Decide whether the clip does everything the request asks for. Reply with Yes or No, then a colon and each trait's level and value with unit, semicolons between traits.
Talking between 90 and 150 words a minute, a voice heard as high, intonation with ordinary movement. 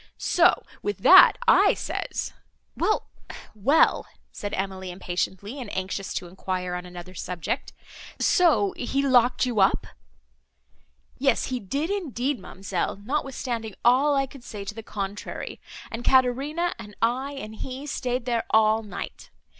No: slow, 135 wpm; high, 230 Hz; wide, 5.7 semitones